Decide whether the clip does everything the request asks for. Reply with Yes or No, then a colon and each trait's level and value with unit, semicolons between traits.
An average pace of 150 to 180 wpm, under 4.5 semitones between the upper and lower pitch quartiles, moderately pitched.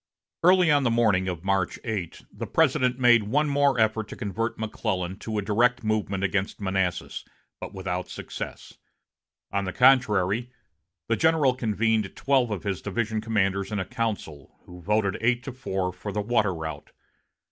No: average, 165 wpm; average, 4.0 semitones; low, 110 Hz